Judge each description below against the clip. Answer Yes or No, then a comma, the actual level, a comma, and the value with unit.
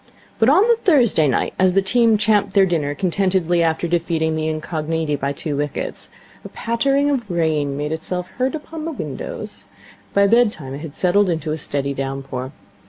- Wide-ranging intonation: Yes, wide, 6.5 semitones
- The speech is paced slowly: No, average, 175 wpm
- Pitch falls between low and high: Yes, medium, 170 Hz